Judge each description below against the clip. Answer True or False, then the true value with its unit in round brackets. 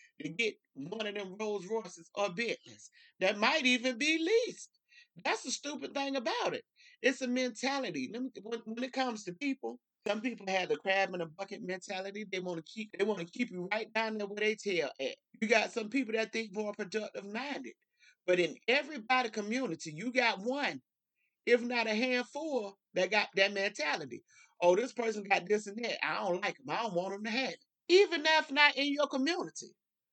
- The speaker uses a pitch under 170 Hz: False (230 Hz)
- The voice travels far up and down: False (5.0 semitones)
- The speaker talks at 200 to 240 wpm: True (205 wpm)